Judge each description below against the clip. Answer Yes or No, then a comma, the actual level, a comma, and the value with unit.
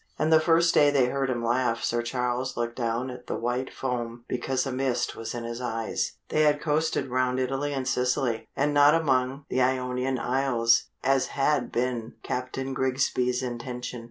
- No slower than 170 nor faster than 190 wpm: Yes, average, 180 wpm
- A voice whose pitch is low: Yes, low, 130 Hz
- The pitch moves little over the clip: Yes, narrow, 1.9 semitones